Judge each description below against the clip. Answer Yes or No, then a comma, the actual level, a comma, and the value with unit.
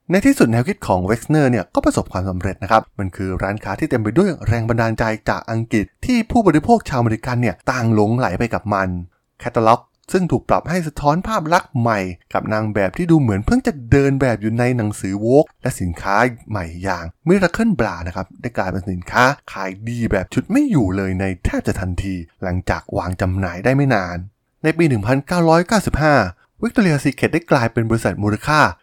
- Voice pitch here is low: Yes, low, 115 Hz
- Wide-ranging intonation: Yes, wide, 7.0 semitones